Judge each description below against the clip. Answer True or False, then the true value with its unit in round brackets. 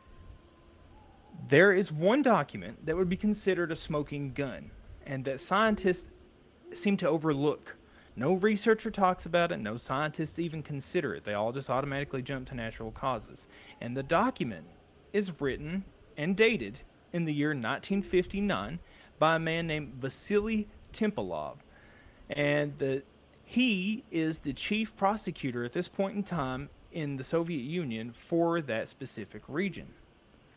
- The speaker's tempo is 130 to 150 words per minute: True (140 wpm)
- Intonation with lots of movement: True (6.1 semitones)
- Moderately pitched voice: True (160 Hz)